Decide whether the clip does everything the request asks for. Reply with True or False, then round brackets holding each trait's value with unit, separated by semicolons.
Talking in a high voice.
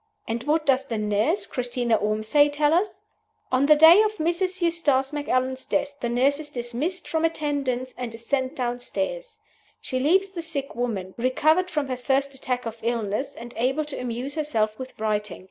True (265 Hz)